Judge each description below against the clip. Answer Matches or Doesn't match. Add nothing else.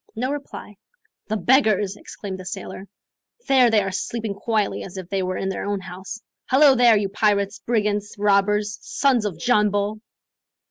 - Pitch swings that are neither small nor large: Doesn't match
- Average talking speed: Matches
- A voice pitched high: Matches